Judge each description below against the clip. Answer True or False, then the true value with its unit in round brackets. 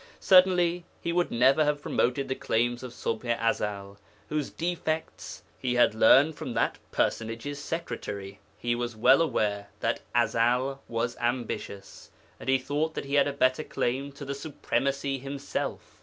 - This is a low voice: True (130 Hz)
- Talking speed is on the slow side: False (155 wpm)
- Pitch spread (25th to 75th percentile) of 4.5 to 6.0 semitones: False (3.6 semitones)